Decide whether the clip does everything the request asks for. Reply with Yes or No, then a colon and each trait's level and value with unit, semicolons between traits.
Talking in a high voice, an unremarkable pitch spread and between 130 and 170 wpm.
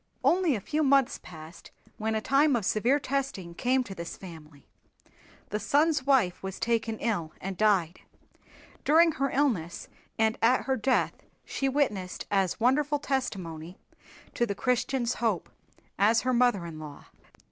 No: high, 225 Hz; wide, 6.5 semitones; average, 150 wpm